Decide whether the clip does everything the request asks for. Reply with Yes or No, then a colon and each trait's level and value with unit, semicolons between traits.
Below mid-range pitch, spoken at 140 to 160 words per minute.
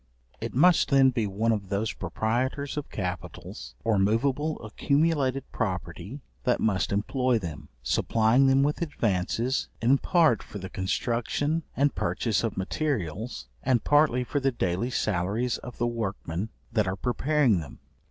Yes: low, 115 Hz; average, 145 wpm